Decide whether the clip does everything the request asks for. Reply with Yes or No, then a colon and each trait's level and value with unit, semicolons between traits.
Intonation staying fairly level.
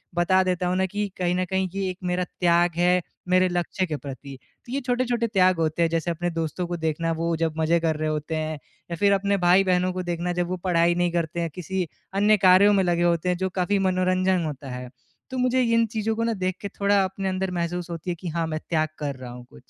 Yes: narrow, 2.3 semitones